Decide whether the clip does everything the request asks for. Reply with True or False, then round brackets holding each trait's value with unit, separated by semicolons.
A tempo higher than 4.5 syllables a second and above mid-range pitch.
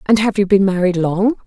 True (5.5 syllables/s; 195 Hz)